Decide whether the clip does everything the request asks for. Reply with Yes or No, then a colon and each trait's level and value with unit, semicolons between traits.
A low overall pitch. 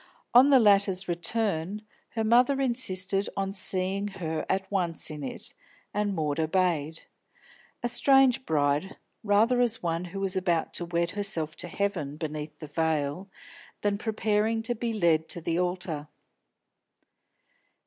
No: medium, 185 Hz